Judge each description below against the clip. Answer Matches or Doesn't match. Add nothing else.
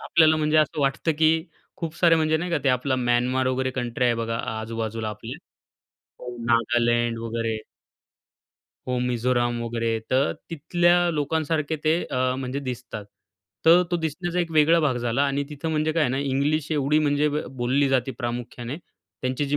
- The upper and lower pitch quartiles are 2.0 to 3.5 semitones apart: Doesn't match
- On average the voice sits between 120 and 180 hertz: Matches